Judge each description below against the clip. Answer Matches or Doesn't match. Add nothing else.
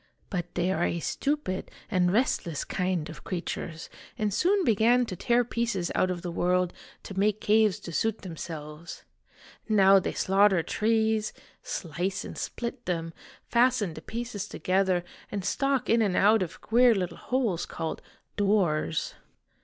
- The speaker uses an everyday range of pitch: Matches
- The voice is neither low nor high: Doesn't match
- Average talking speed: Matches